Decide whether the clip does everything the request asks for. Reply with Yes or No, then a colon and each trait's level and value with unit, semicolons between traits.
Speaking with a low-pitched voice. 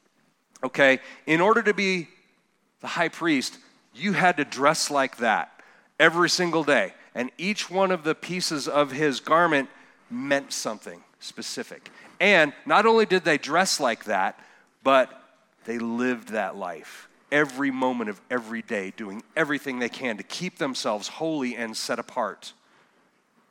No: medium, 155 Hz